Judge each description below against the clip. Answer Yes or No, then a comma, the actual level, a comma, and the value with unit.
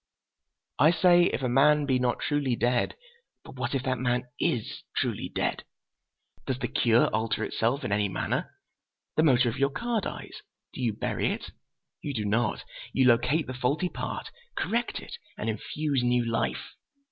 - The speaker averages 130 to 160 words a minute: No, average, 170 wpm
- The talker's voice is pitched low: Yes, low, 130 Hz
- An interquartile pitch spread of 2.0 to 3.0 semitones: No, average, 3.5 semitones